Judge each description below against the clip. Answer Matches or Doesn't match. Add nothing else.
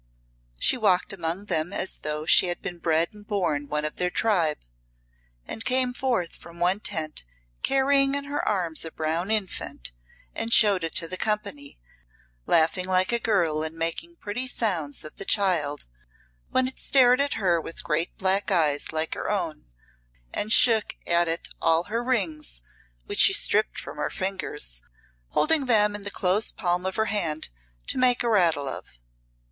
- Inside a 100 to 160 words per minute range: Doesn't match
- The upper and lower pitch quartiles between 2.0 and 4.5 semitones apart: Doesn't match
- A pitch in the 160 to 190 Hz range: Matches